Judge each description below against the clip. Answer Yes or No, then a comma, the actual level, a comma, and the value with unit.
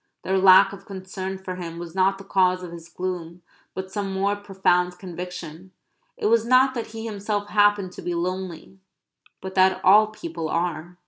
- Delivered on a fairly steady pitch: Yes, narrow, 2.0 semitones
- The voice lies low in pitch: No, high, 190 Hz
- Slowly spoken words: No, average, 180 wpm